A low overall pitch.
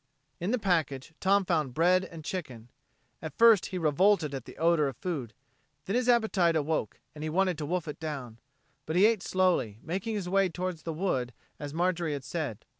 No: medium, 170 Hz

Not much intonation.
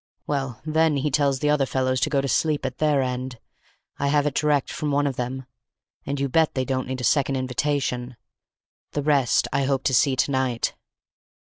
Yes: narrow, 2.1 semitones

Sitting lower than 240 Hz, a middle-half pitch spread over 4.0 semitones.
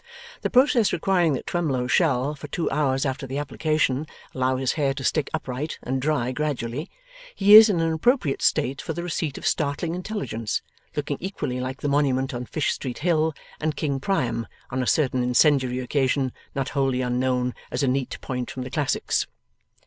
No: medium, 140 Hz; average, 3.5 semitones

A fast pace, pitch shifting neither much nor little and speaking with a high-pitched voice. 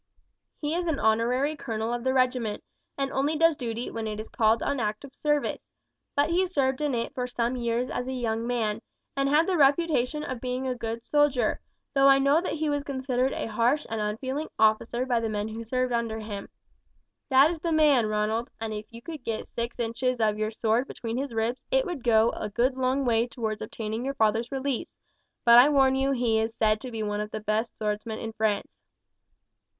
Yes: fast, 210 wpm; average, 3.6 semitones; high, 245 Hz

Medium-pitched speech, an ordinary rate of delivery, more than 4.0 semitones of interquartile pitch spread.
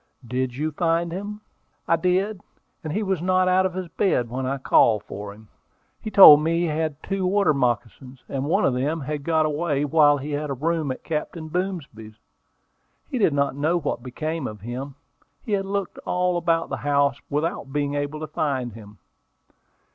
Yes: medium, 150 Hz; average, 185 wpm; average, 4.4 semitones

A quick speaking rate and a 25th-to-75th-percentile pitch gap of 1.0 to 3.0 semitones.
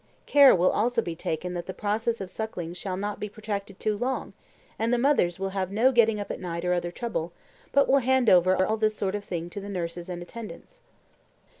No: fast, 220 wpm; average, 4.2 semitones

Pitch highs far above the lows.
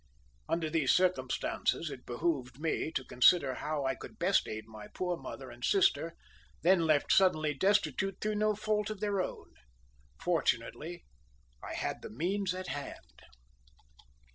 Yes: wide, 6.2 semitones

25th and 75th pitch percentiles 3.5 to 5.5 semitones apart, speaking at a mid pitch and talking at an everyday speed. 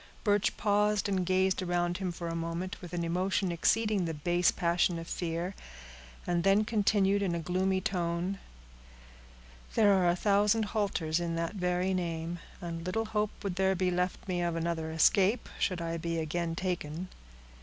No: narrow, 2.5 semitones; medium, 180 Hz; average, 170 wpm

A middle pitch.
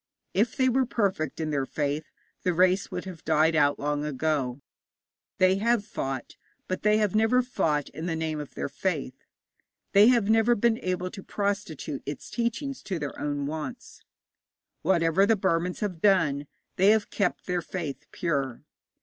Yes: medium, 180 Hz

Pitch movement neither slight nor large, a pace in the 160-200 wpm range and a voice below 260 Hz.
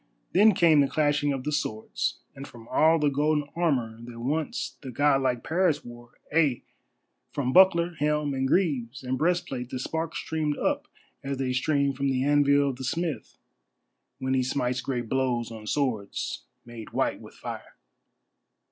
Yes: average, 3.2 semitones; average, 165 wpm; medium, 140 Hz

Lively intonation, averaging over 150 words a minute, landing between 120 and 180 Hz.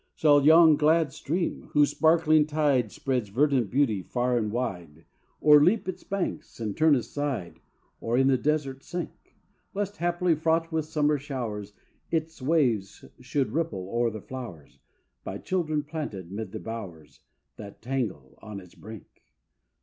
No: wide, 6.3 semitones; average, 145 wpm; low, 135 Hz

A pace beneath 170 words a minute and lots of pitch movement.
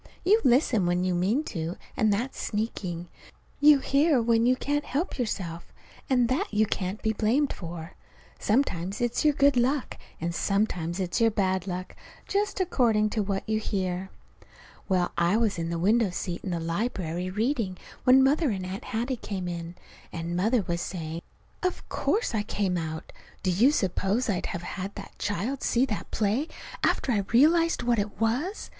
No: average, 175 wpm; wide, 5.7 semitones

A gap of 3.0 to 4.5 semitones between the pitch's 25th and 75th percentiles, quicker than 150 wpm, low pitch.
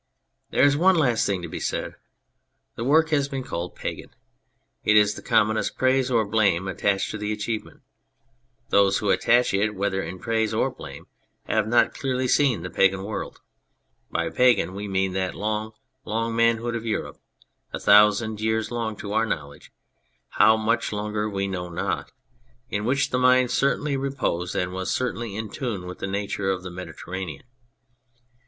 Yes: average, 3.6 semitones; average, 175 wpm; low, 110 Hz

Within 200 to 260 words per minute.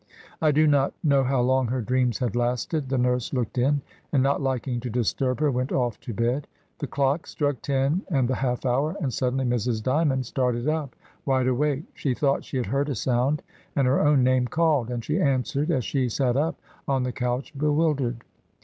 Yes: fast, 205 wpm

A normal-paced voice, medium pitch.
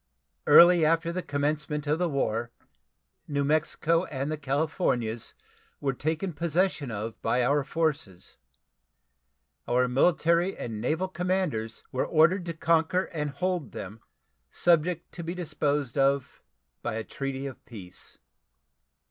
No: slow, 130 wpm; medium, 150 Hz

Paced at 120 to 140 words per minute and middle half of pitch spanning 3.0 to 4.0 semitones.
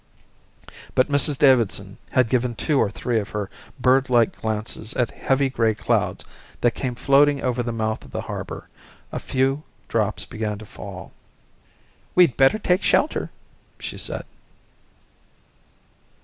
Yes: slow, 135 wpm; average, 3.6 semitones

